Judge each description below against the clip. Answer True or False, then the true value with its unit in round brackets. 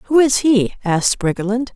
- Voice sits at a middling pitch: False (230 Hz)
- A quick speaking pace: False (170 wpm)